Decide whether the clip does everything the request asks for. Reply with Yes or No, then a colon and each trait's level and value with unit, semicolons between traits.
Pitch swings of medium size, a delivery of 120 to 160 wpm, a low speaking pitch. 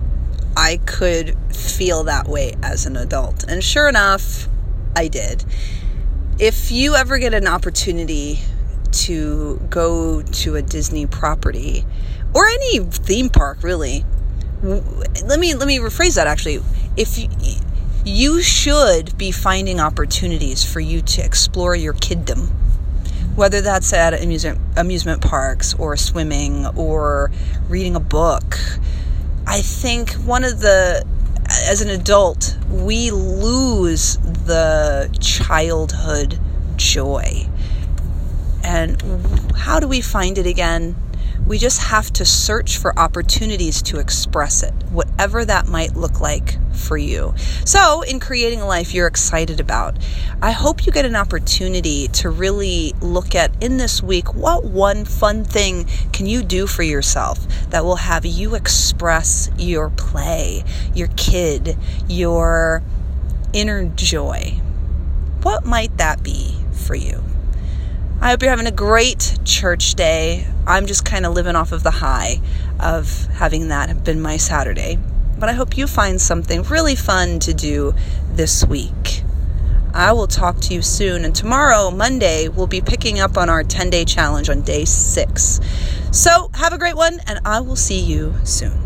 Yes: average, 4.5 semitones; average, 145 wpm; very low, 75 Hz